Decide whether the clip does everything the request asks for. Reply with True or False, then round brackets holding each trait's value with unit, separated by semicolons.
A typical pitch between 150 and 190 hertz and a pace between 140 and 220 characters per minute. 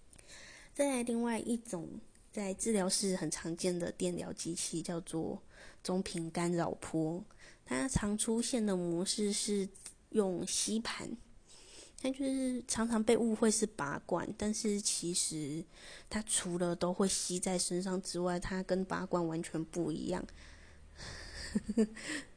True (185 Hz; 190 characters per minute)